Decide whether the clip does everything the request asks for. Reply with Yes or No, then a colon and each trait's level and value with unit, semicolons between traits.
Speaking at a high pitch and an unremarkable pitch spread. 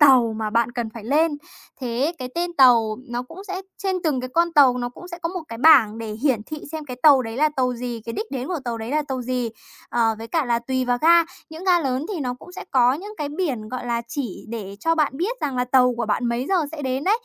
Yes: very high, 255 Hz; average, 5.0 semitones